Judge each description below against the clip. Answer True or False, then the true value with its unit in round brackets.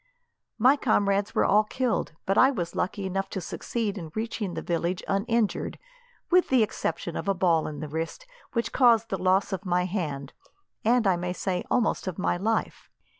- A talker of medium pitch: False (195 Hz)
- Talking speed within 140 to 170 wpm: False (185 wpm)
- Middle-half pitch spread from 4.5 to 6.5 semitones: False (4.1 semitones)